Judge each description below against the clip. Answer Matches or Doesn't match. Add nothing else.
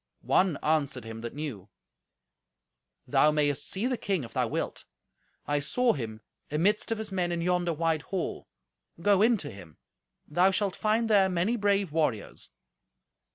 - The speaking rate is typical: Matches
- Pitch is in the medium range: Matches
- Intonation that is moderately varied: Doesn't match